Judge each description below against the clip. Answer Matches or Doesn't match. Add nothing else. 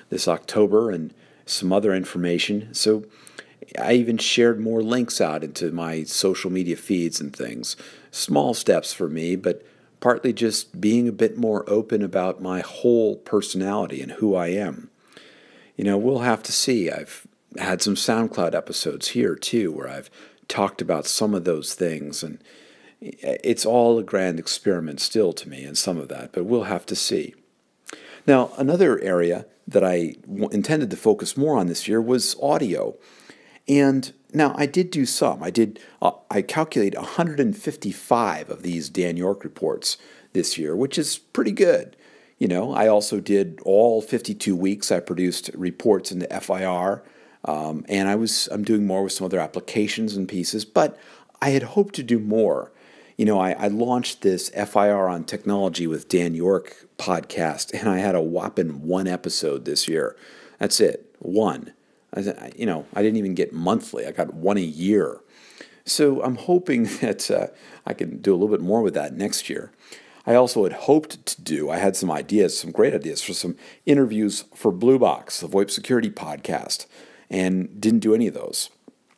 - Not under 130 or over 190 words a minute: Matches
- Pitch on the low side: Matches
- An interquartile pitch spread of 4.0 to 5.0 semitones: Matches